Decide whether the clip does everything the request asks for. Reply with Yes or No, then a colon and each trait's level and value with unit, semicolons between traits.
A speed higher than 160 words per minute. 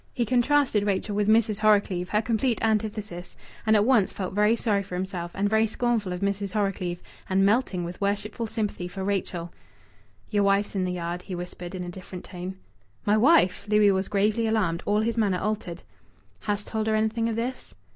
Yes: average, 190 wpm